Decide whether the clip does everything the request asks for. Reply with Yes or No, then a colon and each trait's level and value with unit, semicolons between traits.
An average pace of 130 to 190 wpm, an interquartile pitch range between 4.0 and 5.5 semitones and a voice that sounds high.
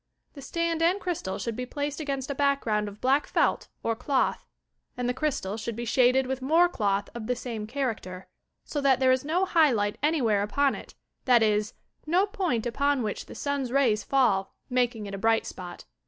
No: average, 200 wpm; average, 4.8 semitones; very high, 255 Hz